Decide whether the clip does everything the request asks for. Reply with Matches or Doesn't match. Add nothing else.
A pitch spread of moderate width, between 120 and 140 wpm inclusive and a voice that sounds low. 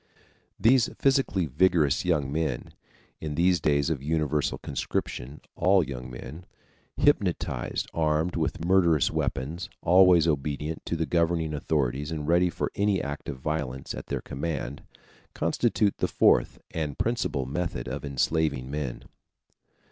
Matches